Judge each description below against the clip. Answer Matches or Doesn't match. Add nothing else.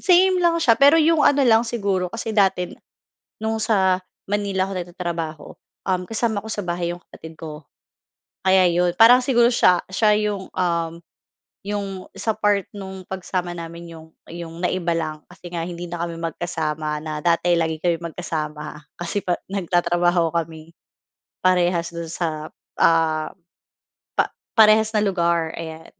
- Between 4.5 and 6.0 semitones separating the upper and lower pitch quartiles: Doesn't match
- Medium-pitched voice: Matches